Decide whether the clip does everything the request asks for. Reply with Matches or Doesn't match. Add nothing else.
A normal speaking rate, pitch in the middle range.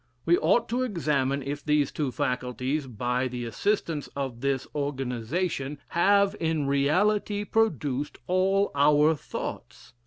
Doesn't match